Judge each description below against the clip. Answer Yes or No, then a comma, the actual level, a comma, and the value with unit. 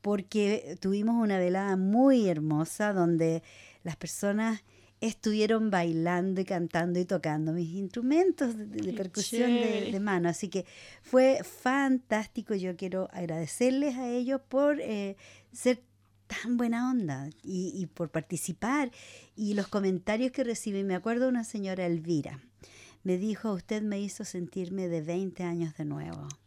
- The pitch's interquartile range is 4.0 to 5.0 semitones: Yes, average, 4.7 semitones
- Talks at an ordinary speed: Yes, average, 145 wpm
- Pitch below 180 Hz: No, high, 195 Hz